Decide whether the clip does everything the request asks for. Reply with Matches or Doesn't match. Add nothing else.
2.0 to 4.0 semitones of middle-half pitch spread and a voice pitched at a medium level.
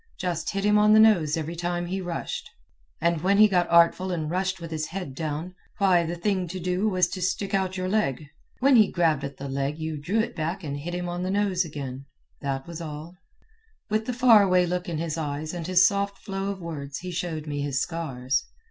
Matches